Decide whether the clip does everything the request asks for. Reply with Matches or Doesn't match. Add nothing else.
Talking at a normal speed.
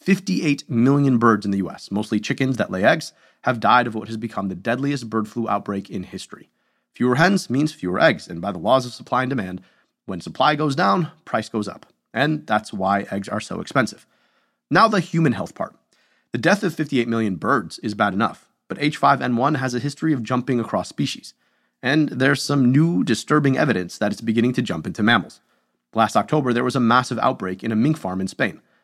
Doesn't match